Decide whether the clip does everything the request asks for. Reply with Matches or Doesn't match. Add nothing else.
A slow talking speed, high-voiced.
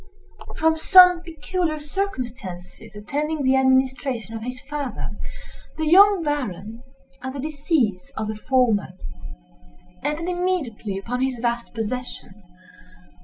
Matches